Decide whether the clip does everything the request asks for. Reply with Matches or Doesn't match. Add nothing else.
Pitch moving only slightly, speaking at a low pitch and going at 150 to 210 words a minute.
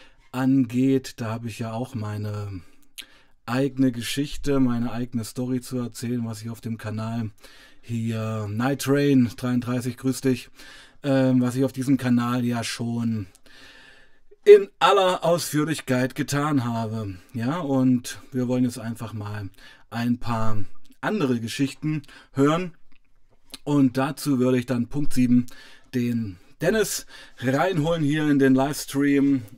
Doesn't match